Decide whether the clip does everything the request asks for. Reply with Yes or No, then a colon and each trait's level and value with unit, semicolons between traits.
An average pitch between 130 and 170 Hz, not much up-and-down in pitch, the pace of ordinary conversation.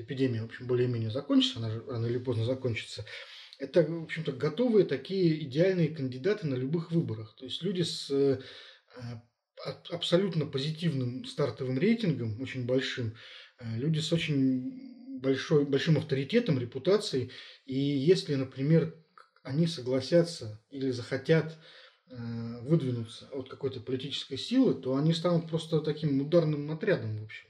No: low, 135 Hz; average, 4.3 semitones; average, 130 wpm